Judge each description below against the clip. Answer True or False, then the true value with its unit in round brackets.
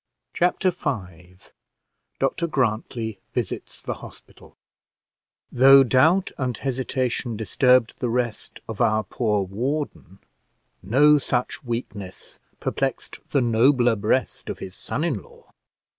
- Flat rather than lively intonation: False (3.8 semitones)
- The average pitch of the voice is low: True (125 Hz)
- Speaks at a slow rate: True (115 wpm)